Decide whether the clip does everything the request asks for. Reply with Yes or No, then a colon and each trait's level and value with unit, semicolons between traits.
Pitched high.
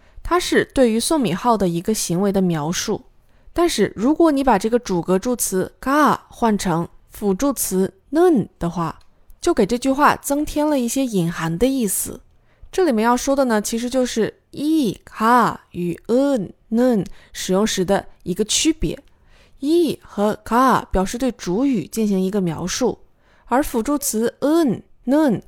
Yes: high, 230 Hz